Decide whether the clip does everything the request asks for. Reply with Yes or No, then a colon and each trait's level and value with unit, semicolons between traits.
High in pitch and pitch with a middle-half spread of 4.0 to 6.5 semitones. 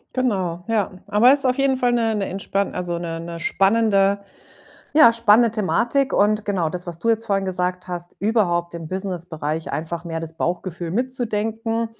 Yes: high, 195 Hz; average, 4.6 semitones